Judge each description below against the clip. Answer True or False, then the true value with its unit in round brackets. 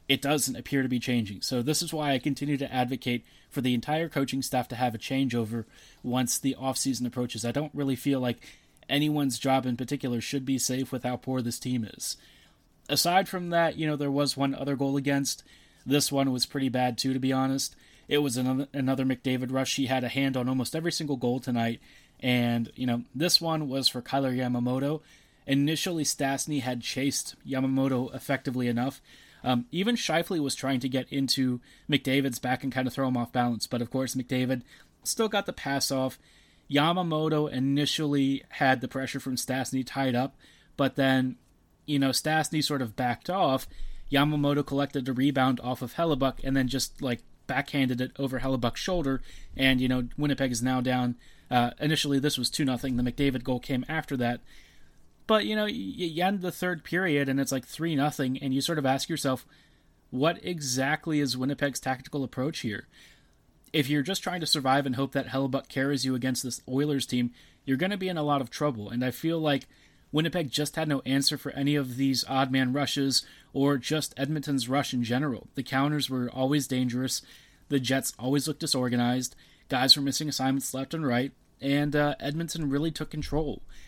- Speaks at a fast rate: False (195 wpm)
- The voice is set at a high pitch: False (135 Hz)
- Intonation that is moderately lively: False (2.2 semitones)